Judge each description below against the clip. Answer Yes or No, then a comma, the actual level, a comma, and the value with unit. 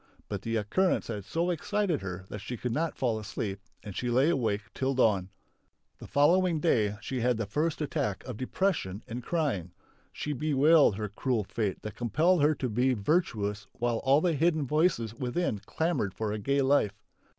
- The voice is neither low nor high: No, low, 125 Hz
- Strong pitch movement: Yes, wide, 6.6 semitones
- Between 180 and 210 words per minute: Yes, average, 185 wpm